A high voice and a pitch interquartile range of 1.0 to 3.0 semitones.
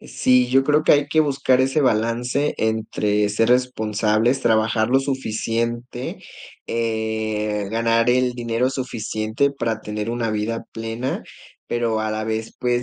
No: low, 115 Hz; narrow, 2.5 semitones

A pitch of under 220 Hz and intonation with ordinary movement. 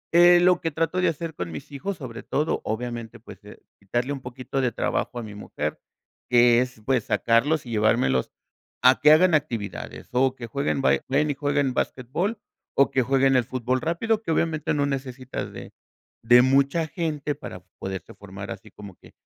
Yes: low, 135 Hz; average, 4.2 semitones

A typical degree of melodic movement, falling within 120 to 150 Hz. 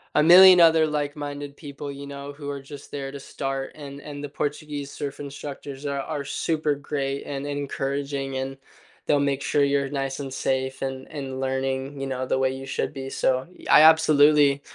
No: narrow, 1.2 semitones; medium, 140 Hz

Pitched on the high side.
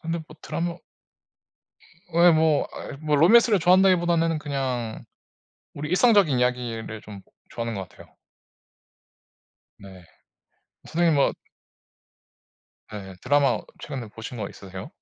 No: medium, 145 Hz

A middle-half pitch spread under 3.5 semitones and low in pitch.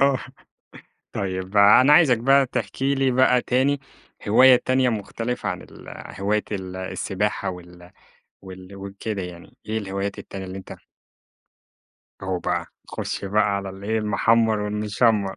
No: average, 4.3 semitones; low, 105 Hz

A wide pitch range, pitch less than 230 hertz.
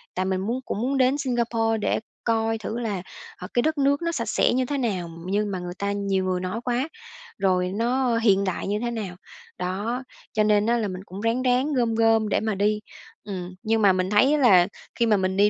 No: average, 3.9 semitones; high, 220 Hz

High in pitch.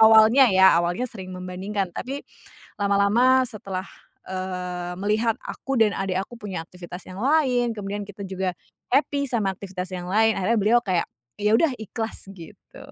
Yes: high, 200 Hz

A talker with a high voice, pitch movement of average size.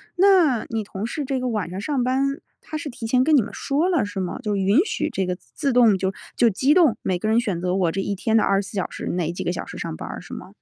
No: high, 225 Hz; wide, 6.1 semitones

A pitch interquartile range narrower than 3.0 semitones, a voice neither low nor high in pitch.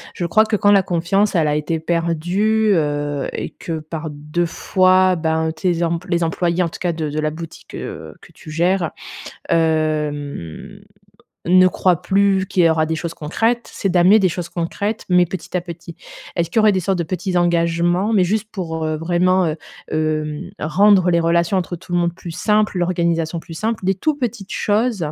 Yes: narrow, 2.6 semitones; medium, 175 Hz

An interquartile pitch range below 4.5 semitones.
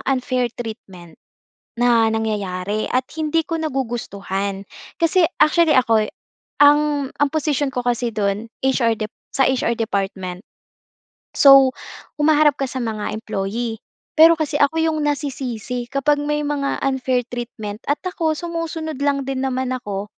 No: average, 4.8 semitones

